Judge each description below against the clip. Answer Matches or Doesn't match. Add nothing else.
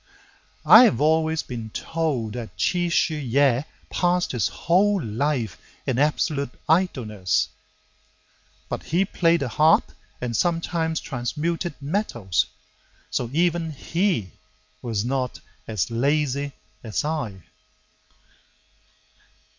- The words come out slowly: Matches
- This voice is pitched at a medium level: Matches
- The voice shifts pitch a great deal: Matches